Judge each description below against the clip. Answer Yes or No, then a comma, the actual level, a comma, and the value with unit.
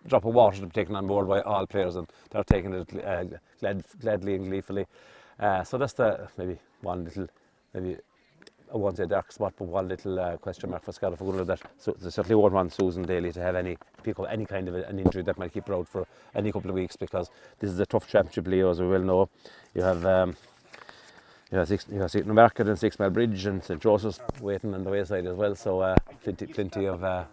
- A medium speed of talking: No, fast, 245 wpm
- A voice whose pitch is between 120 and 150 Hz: No, very low, 95 Hz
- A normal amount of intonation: No, narrow, 1.8 semitones